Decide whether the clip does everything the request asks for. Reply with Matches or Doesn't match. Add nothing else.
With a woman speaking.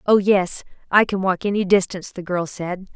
Matches